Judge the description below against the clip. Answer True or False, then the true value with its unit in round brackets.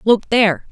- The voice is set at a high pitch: True (210 Hz)